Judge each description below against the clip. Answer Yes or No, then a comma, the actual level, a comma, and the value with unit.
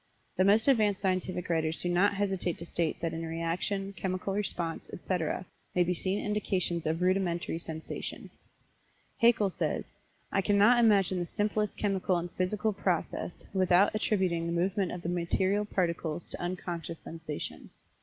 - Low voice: No, medium, 185 Hz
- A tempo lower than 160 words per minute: Yes, average, 150 wpm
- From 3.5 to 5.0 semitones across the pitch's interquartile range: No, average, 2.8 semitones